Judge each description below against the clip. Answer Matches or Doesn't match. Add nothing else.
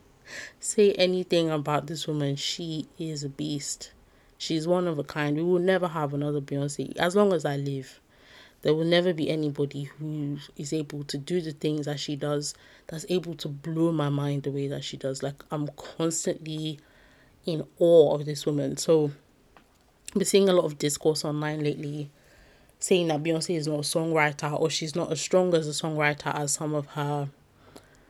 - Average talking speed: Matches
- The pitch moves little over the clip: Matches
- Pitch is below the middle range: Doesn't match